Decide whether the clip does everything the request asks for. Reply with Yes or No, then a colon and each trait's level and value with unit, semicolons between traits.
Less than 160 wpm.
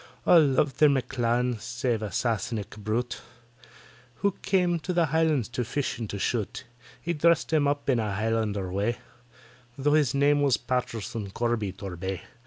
No: average, 165 wpm